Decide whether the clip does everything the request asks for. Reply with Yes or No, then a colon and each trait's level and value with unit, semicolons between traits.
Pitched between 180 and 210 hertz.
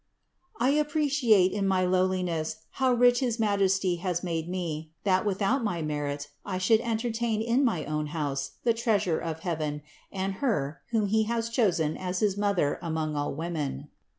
Yes: medium, 185 Hz